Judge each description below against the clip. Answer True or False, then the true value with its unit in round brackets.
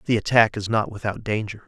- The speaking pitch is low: True (110 Hz)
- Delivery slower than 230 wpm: True (215 wpm)